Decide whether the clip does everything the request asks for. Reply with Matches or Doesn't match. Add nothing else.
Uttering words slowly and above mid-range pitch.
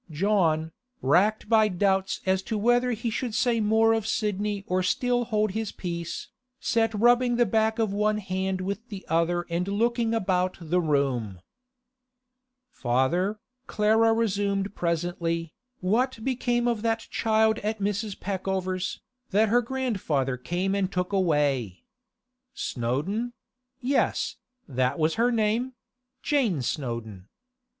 Matches